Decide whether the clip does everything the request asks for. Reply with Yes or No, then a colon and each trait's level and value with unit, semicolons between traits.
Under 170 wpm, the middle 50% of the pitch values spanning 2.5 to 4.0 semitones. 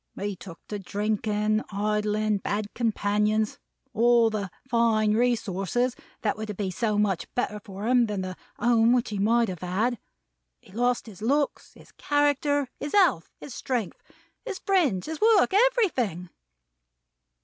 Yes: average, 145 wpm; average, 3.2 semitones